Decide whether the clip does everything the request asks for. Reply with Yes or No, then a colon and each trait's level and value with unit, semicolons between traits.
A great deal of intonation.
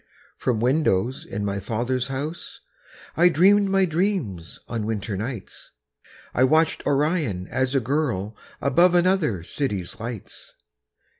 Yes: wide, 7.0 semitones